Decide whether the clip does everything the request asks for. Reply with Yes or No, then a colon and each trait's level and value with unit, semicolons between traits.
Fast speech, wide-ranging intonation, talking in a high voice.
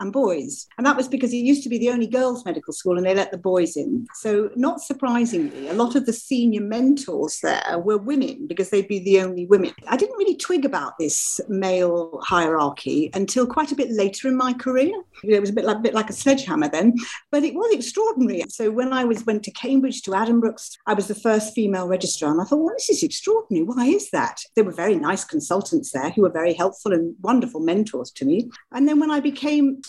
Yes: fast, 230 wpm; wide, 6.2 semitones; high, 235 Hz